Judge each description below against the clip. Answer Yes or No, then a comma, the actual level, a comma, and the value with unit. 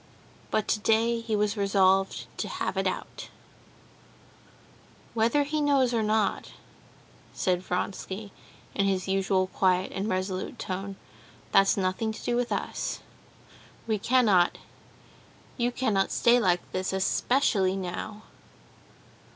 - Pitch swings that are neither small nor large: Yes, average, 3.4 semitones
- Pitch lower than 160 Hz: No, high, 200 Hz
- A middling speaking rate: No, slow, 120 wpm